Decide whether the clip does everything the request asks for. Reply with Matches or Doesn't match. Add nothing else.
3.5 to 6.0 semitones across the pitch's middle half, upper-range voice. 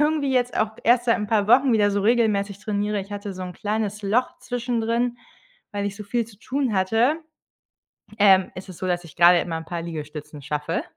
Matches